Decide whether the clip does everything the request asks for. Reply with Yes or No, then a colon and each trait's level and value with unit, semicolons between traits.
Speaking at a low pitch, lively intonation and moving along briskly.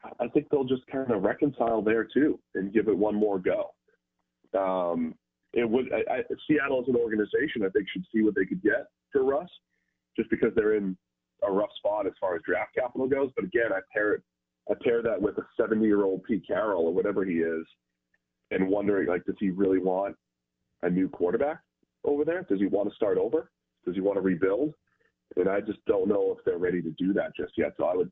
Yes: low, 100 Hz; wide, 6.3 semitones; fast, 225 wpm